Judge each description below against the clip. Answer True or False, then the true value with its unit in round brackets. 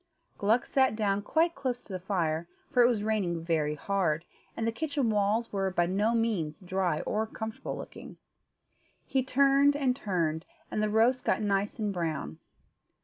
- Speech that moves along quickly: False (170 wpm)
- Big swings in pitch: False (5.0 semitones)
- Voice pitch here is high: True (210 Hz)